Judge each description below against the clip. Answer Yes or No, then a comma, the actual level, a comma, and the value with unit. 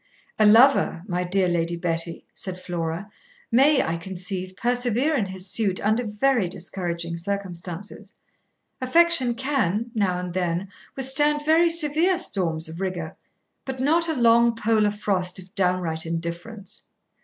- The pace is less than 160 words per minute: Yes, slow, 135 wpm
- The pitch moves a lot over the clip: Yes, wide, 5.9 semitones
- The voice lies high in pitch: Yes, high, 195 Hz